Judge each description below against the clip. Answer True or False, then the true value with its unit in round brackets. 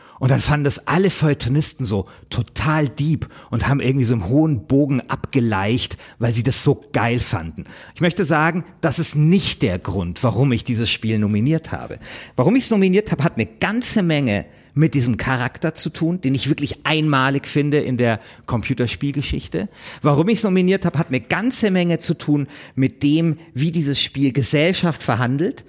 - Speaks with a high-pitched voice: False (140 Hz)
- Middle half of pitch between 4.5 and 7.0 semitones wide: True (4.9 semitones)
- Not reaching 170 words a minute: False (180 wpm)